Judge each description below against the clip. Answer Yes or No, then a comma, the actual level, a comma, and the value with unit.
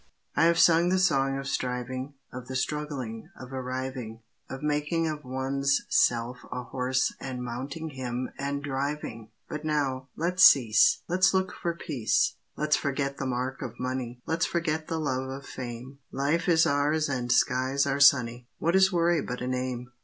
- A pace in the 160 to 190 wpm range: Yes, average, 170 wpm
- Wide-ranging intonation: No, average, 3.2 semitones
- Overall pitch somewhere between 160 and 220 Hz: No, low, 135 Hz